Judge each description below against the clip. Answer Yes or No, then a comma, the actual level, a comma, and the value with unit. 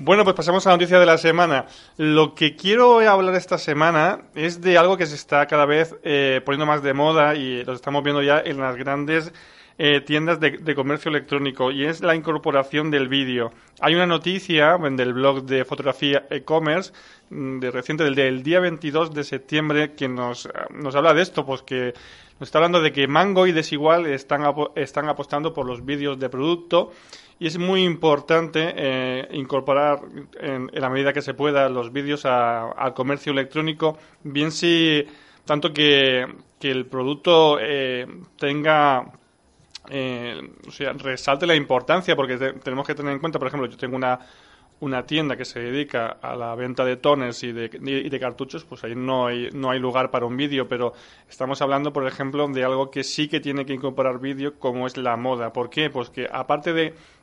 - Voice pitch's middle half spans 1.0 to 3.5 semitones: Yes, average, 3.1 semitones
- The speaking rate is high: Yes, fast, 195 wpm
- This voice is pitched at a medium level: Yes, medium, 145 Hz